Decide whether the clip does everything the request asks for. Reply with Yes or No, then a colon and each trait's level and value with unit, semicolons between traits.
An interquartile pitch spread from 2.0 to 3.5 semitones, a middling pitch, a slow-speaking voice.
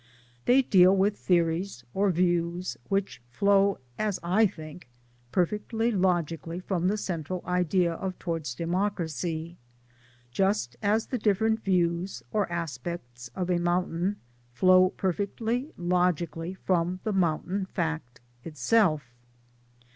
Yes: average, 2.9 semitones; medium, 180 Hz; slow, 115 wpm